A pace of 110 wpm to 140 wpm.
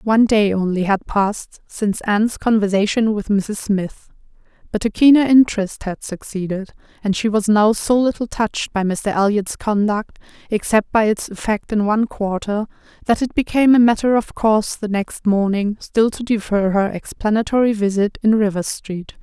No: average, 170 wpm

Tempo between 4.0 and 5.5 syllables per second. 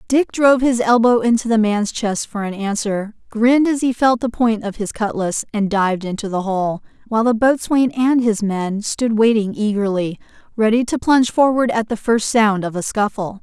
Yes: 5.0 syllables/s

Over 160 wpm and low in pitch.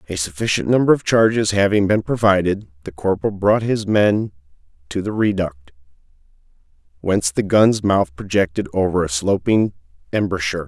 No: average, 140 wpm; very low, 95 Hz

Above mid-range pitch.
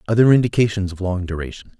No: low, 100 Hz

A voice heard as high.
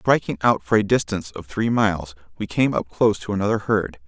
No: low, 100 Hz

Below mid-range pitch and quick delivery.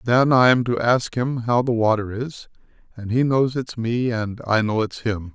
Yes: low, 120 Hz; fast, 225 wpm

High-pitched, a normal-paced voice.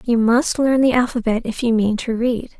No: high, 235 Hz; fast, 230 wpm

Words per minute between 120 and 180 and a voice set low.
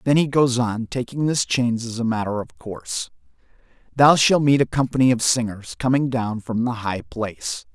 No: average, 195 wpm; low, 120 Hz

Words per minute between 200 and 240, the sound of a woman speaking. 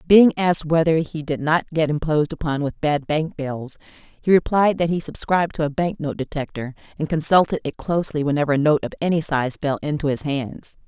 Yes: fast, 205 wpm; female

